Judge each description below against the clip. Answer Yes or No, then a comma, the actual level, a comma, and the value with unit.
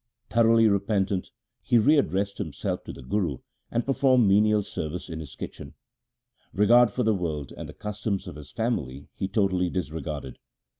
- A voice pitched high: No, low, 100 Hz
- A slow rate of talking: No, average, 160 wpm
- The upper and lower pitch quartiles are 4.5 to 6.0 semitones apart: Yes, wide, 5.6 semitones